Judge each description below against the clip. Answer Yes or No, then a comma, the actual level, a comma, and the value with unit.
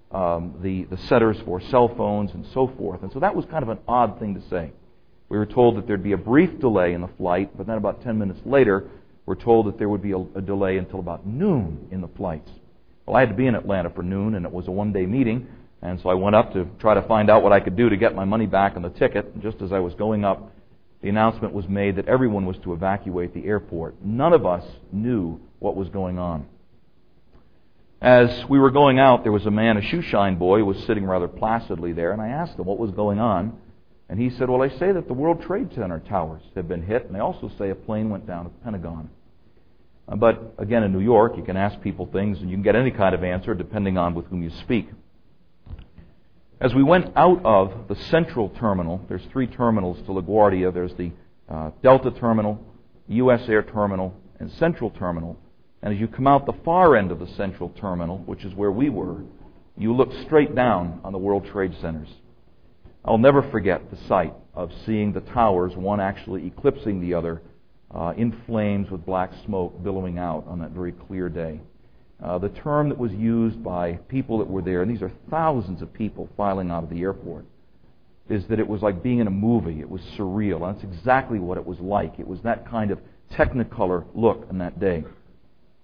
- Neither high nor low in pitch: No, low, 100 Hz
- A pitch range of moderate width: Yes, average, 4.0 semitones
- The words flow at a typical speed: No, fast, 225 wpm